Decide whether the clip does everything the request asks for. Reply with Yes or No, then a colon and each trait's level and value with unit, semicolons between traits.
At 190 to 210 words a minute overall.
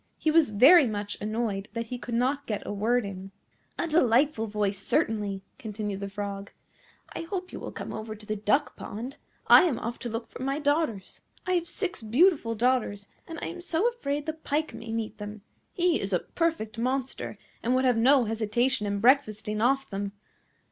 Yes: average, 195 wpm